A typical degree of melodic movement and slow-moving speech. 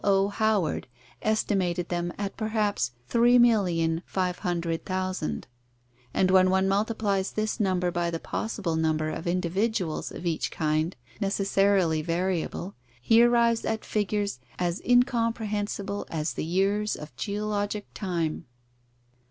Yes: average, 3.6 semitones; slow, 110 wpm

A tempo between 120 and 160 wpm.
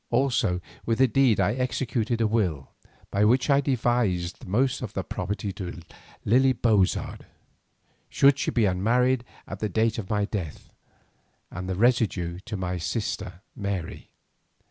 Yes: average, 150 wpm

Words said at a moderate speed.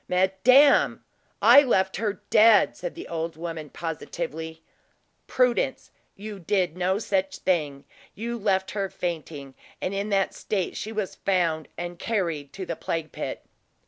Yes: average, 145 wpm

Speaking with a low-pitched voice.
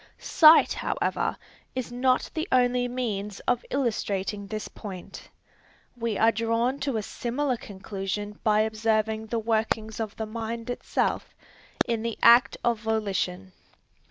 No: high, 225 Hz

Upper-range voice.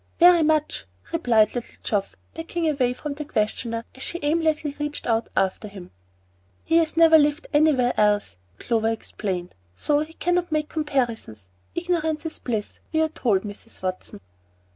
Yes: very high, 290 Hz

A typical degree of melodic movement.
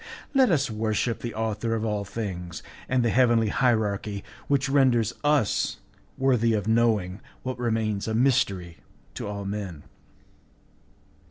Yes: average, 3.3 semitones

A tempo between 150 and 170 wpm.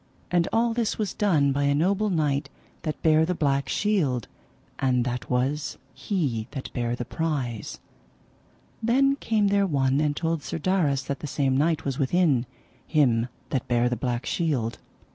Yes: average, 165 wpm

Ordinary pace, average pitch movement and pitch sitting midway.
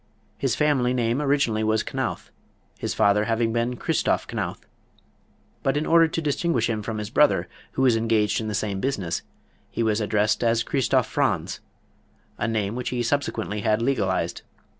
No: average, 165 wpm; average, 3.6 semitones; low, 115 Hz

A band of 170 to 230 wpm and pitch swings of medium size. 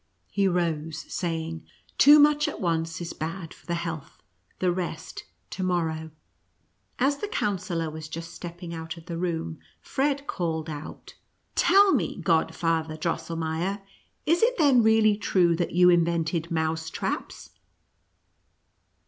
No: average, 150 wpm; average, 3.1 semitones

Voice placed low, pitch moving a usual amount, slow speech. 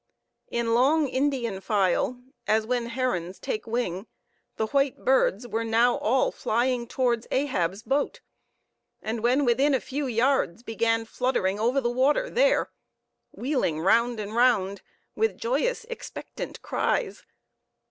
No: high, 240 Hz; average, 3.3 semitones; slow, 130 wpm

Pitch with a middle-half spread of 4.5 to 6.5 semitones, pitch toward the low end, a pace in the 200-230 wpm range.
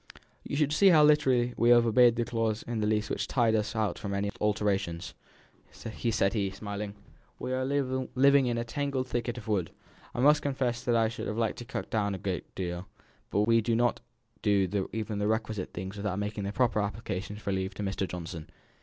No: average, 3.2 semitones; low, 110 Hz; fast, 205 wpm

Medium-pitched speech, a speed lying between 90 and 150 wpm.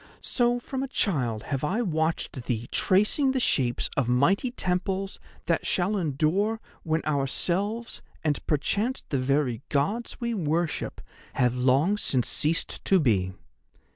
Yes: medium, 160 Hz; average, 140 wpm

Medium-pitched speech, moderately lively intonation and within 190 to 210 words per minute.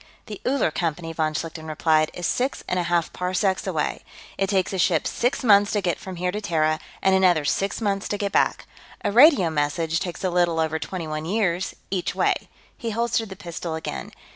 Yes: medium, 180 Hz; average, 3.7 semitones; fast, 205 wpm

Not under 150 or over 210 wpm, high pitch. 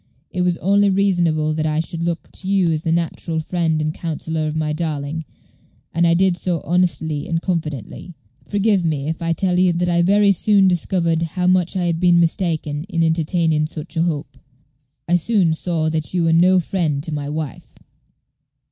No: average, 190 wpm; medium, 170 Hz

